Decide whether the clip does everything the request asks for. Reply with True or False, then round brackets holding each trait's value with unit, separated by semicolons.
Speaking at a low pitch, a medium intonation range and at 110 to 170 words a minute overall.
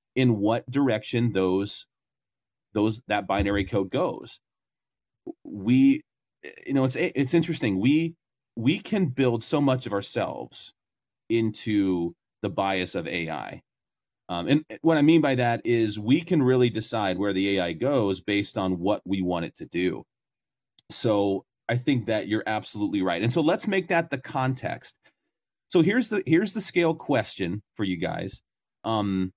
False (120 Hz; 7.5 semitones; 155 wpm)